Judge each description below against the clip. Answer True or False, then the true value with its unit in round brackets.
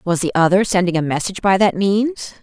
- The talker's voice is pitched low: False (190 Hz)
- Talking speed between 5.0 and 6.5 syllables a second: True (5.9 syllables/s)